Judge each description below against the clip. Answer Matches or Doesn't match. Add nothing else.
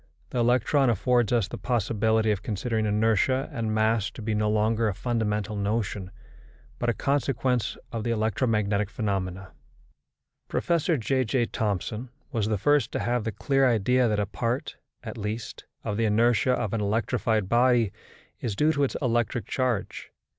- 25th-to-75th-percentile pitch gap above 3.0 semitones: Doesn't match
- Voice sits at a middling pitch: Doesn't match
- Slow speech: Doesn't match